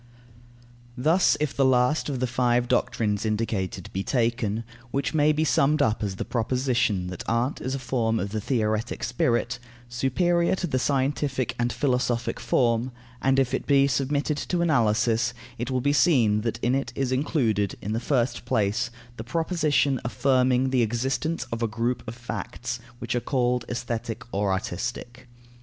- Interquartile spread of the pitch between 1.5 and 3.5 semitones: Yes, average, 2.9 semitones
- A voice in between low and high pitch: No, low, 125 Hz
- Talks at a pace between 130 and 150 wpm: No, average, 165 wpm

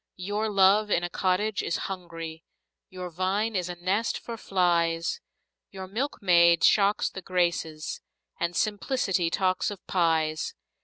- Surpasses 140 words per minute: No, slow, 135 wpm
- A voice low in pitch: No, medium, 185 Hz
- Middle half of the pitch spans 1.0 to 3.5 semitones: Yes, average, 2.9 semitones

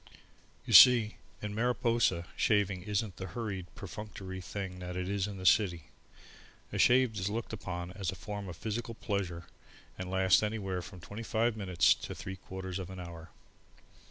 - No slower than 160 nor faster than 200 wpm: Yes, average, 170 wpm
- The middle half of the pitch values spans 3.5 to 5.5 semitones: No, average, 2.9 semitones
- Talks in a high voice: No, very low, 95 Hz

